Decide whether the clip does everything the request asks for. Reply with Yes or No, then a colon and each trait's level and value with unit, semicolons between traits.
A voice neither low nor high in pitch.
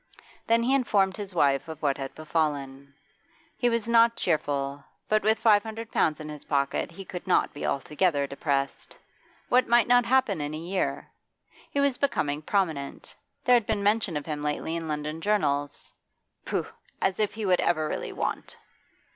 Yes: medium, 170 Hz